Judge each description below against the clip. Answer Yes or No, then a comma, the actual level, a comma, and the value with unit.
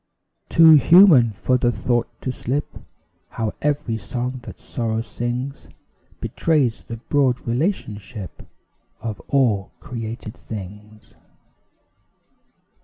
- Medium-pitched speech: No, low, 120 Hz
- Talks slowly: Yes, slow, 100 wpm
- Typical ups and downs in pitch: Yes, average, 3.7 semitones